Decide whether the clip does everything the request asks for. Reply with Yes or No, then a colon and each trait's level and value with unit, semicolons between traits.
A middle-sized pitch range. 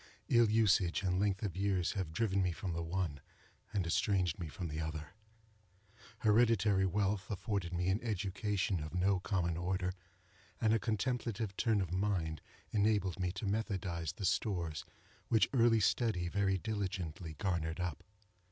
Yes: average, 3.1 semitones